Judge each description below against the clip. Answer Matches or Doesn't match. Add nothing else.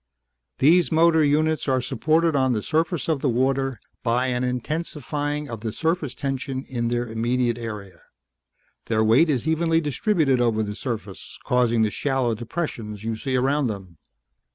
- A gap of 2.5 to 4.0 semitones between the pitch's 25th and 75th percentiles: Doesn't match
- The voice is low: Matches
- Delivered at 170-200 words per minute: Doesn't match